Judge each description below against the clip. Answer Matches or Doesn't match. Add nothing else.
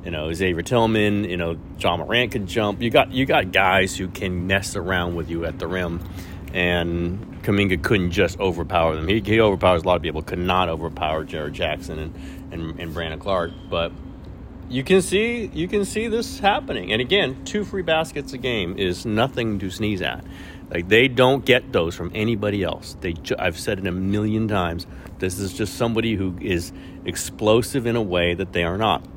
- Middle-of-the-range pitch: Doesn't match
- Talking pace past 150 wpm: Matches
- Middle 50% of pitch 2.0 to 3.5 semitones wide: Doesn't match